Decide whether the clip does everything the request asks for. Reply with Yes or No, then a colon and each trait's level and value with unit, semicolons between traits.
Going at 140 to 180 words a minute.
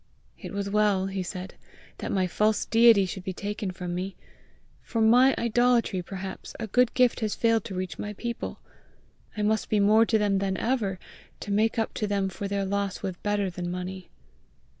No: average, 190 wpm